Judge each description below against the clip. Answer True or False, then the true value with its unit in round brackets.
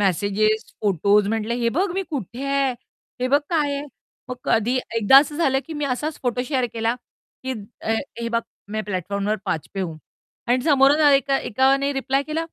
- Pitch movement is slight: False (4.5 semitones)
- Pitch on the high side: True (255 Hz)